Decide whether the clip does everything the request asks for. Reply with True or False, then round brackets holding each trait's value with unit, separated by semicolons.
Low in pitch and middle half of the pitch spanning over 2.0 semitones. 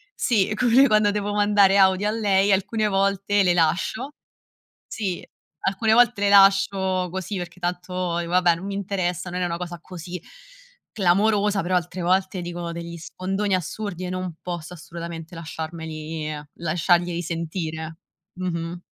False (185 Hz; 2.7 semitones)